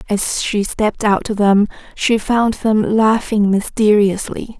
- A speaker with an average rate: Yes, average, 145 wpm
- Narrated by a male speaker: No, female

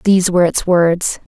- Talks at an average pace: Yes, average, 180 wpm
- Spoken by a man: No, female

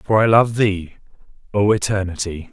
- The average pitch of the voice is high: No, low, 100 Hz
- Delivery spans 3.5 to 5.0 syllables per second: Yes, 4.8 syllables/s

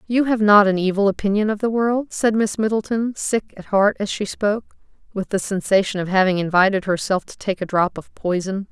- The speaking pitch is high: Yes, high, 205 Hz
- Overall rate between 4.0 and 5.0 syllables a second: No, 5.5 syllables/s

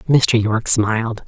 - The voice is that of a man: No, female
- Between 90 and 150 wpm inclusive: Yes, average, 140 wpm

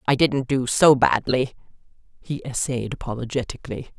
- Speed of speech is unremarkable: No, slow, 120 wpm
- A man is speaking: No, female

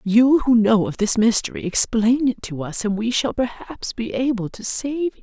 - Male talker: No, female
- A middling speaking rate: No, fast, 220 wpm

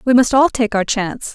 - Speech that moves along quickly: Yes, fast, 265 wpm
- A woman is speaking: Yes, female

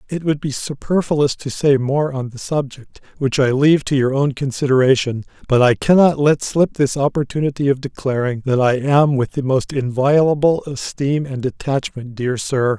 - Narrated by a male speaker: Yes, male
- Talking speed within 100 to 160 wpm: No, average, 180 wpm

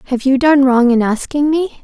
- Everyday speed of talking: No, fast, 230 wpm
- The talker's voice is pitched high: Yes, very high, 270 Hz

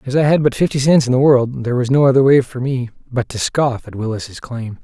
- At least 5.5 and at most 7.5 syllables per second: Yes, 5.8 syllables/s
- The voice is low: Yes, low, 130 Hz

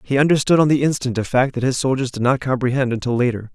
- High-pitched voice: No, low, 130 Hz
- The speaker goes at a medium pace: No, fast, 255 wpm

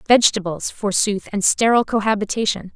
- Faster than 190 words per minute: No, slow, 110 wpm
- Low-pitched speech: No, high, 210 Hz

